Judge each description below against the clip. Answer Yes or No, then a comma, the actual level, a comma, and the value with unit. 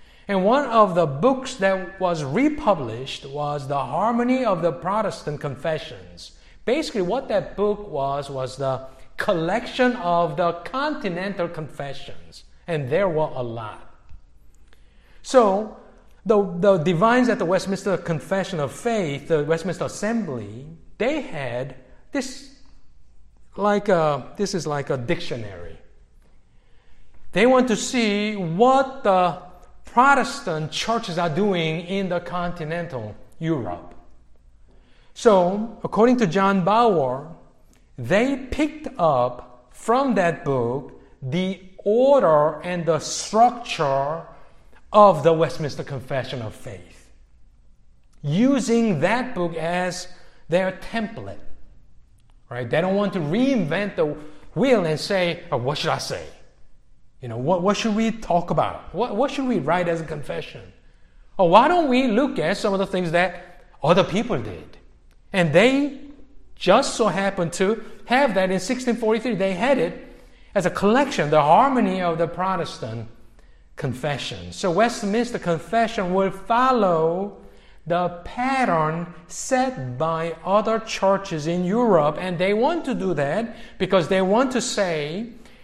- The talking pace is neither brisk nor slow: No, slow, 130 wpm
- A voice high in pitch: No, medium, 180 Hz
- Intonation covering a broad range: Yes, wide, 6.7 semitones